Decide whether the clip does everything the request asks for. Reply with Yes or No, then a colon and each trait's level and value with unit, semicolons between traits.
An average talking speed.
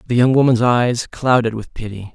Yes: average, 195 wpm